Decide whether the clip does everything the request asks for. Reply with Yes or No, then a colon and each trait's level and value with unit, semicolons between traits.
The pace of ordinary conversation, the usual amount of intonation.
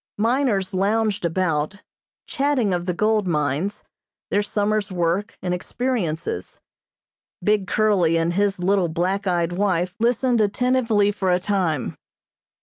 No: slow, 125 wpm; average, 3.3 semitones